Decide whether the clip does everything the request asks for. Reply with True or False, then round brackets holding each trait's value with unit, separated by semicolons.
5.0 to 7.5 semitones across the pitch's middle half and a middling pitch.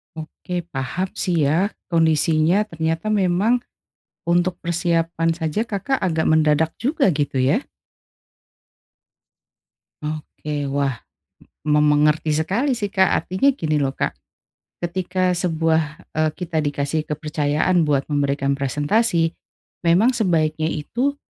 False (3.3 semitones; 160 Hz)